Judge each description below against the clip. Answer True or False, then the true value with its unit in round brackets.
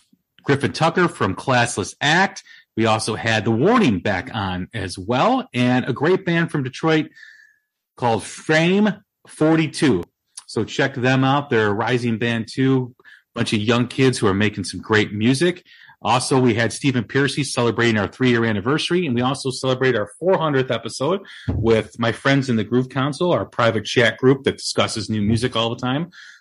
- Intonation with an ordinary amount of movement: True (4.0 semitones)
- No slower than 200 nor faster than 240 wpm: False (175 wpm)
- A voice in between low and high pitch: False (125 Hz)